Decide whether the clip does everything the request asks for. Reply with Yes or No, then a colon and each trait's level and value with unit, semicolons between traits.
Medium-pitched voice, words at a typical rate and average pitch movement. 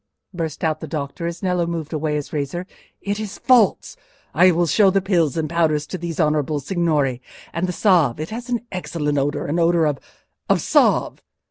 Yes: medium, 165 Hz; average, 175 wpm; average, 3.3 semitones